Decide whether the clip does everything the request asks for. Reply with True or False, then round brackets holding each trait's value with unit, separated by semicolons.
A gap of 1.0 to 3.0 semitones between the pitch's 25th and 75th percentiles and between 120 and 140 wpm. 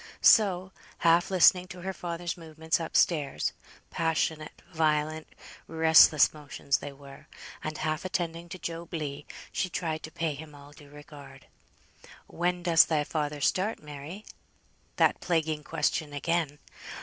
True (2.4 semitones; 135 wpm)